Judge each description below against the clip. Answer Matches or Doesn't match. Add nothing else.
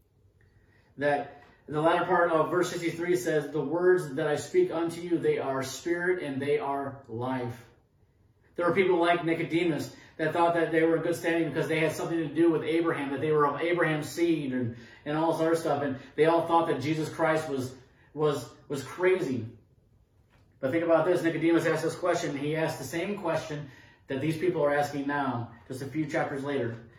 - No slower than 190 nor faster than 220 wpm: Matches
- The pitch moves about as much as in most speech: Matches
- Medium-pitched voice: Matches